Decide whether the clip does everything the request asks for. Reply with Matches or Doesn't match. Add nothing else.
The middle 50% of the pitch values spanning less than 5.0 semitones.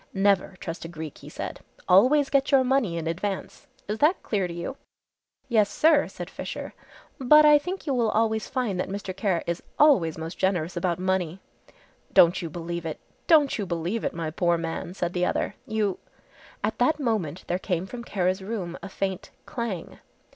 Doesn't match